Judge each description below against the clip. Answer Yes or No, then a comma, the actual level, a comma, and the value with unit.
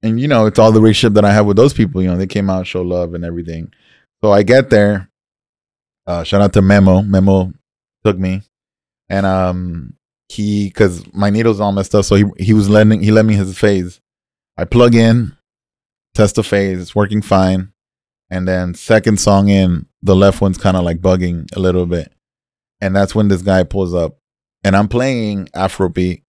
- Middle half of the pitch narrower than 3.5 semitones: Yes, narrow, 2.4 semitones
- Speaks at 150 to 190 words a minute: No, average, 200 wpm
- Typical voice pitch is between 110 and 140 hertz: No, low, 100 Hz